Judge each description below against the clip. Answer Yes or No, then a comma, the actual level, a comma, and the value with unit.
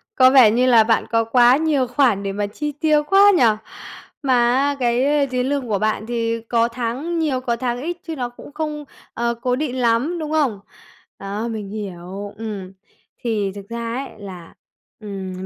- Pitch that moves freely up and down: No, average, 4.4 semitones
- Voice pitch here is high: Yes, high, 240 Hz